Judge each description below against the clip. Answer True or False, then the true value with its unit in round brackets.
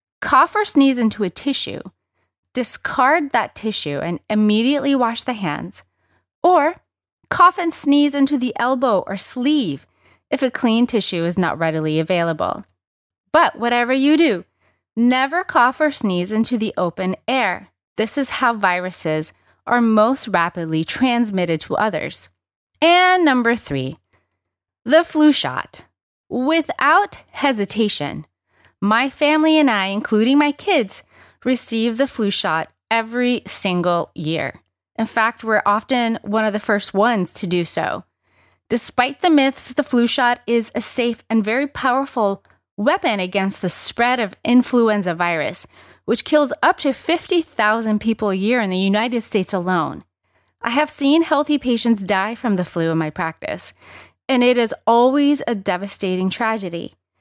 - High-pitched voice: True (230 Hz)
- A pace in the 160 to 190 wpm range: False (145 wpm)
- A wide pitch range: True (6.5 semitones)